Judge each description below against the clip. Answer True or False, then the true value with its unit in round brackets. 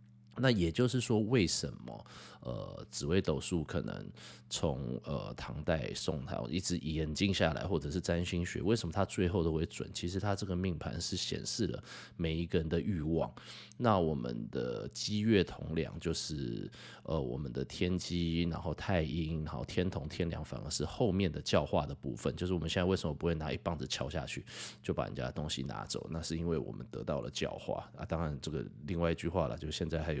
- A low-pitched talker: True (85 Hz)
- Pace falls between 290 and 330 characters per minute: True (300 characters per minute)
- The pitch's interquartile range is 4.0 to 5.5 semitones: False (3.0 semitones)